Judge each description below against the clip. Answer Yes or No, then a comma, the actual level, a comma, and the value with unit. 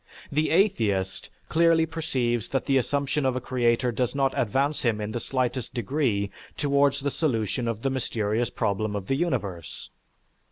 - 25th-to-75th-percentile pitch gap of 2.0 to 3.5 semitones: No, average, 4.2 semitones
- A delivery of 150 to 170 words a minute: Yes, average, 160 wpm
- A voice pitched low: Yes, low, 130 Hz